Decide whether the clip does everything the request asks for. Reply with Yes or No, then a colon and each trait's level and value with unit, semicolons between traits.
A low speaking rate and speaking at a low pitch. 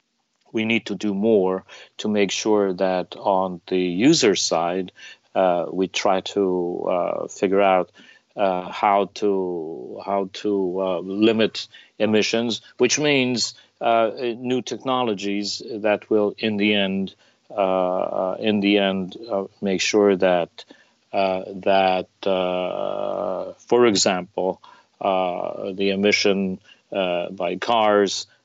Yes: slow, 120 wpm; low, 100 Hz